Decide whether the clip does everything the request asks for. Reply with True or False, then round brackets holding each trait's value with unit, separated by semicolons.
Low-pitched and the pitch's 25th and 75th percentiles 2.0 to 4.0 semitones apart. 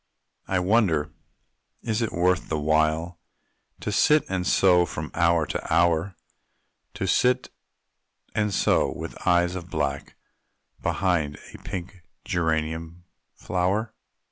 True (85 Hz; 3.0 semitones)